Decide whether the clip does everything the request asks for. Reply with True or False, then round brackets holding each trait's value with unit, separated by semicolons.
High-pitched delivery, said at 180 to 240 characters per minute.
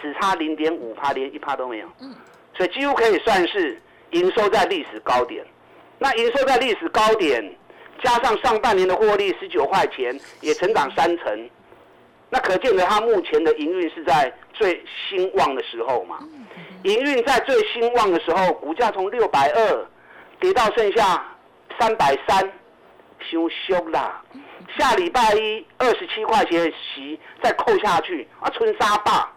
True (345 Hz; 235 characters per minute)